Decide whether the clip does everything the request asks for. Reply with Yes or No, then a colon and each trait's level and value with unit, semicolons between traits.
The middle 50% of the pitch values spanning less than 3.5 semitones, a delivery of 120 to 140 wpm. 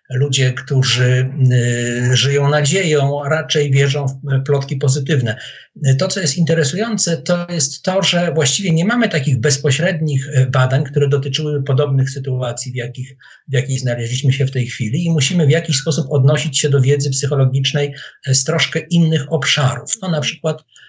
No: average, 3.0 semitones; fast, 160 wpm